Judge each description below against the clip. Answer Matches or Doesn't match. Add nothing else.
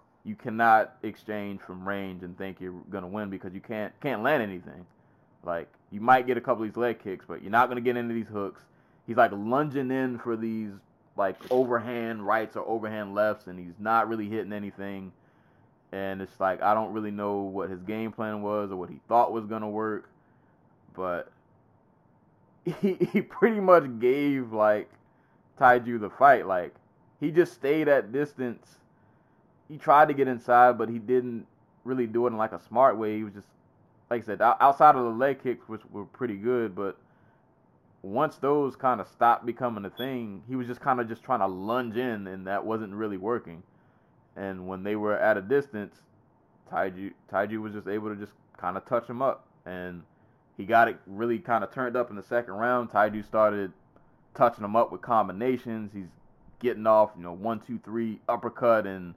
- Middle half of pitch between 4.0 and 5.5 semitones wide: Doesn't match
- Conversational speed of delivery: Matches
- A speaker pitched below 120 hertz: Matches